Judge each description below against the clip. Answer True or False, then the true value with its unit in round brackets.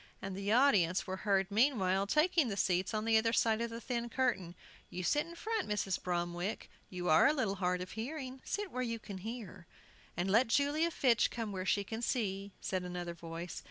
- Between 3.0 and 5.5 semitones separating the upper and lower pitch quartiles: True (5.0 semitones)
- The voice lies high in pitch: True (210 Hz)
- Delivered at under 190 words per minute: False (205 wpm)